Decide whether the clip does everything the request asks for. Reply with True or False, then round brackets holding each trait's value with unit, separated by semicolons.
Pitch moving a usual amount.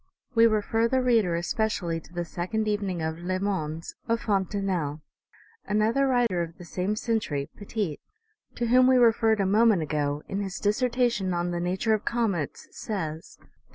True (4.7 semitones)